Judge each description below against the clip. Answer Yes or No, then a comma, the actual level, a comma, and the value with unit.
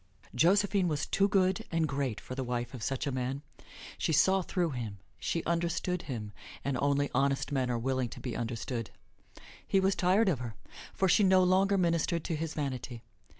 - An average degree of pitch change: No, wide, 6.1 semitones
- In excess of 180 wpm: Yes, average, 190 wpm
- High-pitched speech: No, medium, 145 Hz